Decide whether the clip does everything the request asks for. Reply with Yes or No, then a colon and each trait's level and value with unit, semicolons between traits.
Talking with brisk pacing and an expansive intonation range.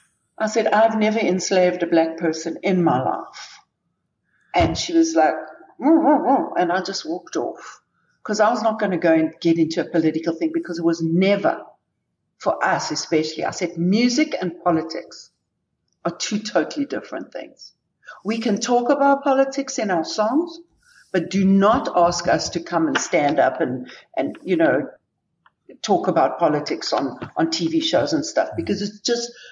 No: average, 175 wpm; wide, 8.2 semitones